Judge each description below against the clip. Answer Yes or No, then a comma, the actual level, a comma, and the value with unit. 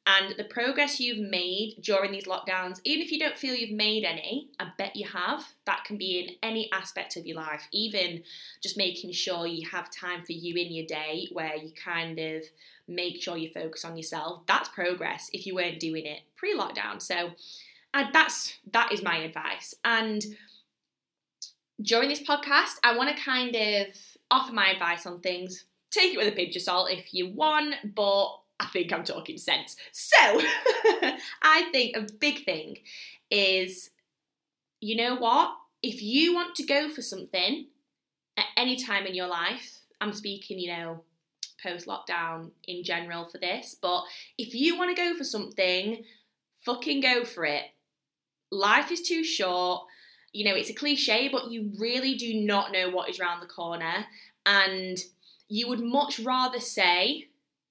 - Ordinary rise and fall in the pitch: No, wide, 6.0 semitones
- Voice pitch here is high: Yes, high, 200 Hz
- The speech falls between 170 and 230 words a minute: Yes, average, 175 wpm